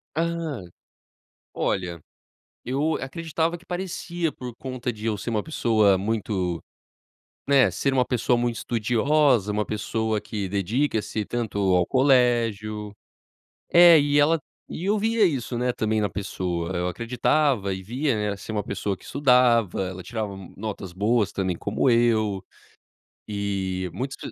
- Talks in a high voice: No, low, 115 Hz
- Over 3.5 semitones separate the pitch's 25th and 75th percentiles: Yes, average, 5.2 semitones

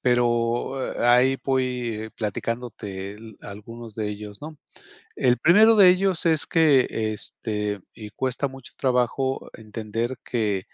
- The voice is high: No, low, 120 Hz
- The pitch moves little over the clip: No, average, 3.7 semitones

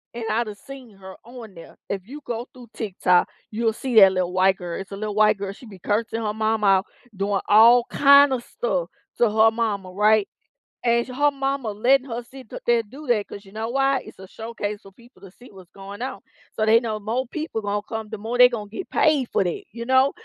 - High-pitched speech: Yes, high, 220 Hz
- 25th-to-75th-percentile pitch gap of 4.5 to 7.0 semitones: No, average, 3.5 semitones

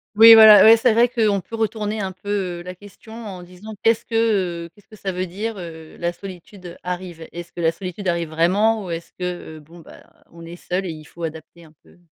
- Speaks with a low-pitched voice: No, medium, 185 Hz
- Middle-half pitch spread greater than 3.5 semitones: Yes, average, 3.9 semitones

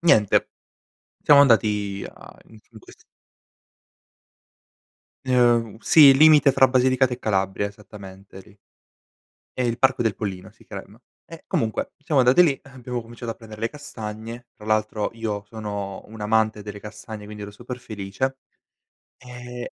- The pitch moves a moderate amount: Yes, average, 3.3 semitones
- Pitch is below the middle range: Yes, low, 110 Hz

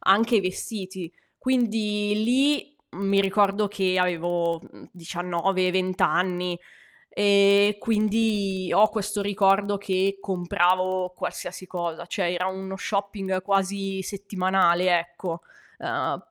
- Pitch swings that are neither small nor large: No, narrow, 2.0 semitones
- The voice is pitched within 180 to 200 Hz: Yes, high, 190 Hz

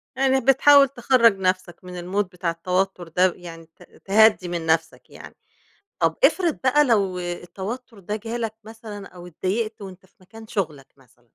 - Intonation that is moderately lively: Yes, average, 4.4 semitones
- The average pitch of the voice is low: No, high, 195 Hz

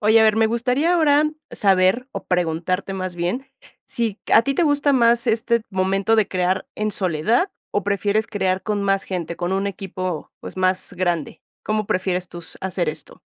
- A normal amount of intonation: Yes, average, 3.7 semitones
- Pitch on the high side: Yes, high, 195 Hz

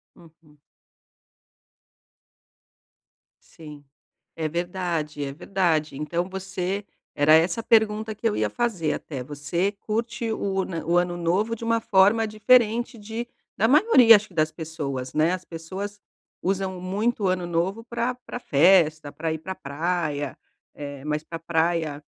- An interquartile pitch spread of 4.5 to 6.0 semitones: Yes, average, 5.1 semitones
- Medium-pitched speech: Yes, medium, 180 Hz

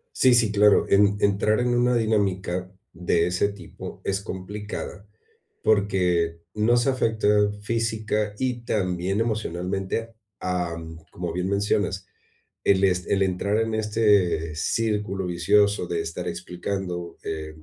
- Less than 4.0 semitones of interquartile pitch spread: Yes, average, 3.2 semitones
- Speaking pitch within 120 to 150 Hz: No, low, 100 Hz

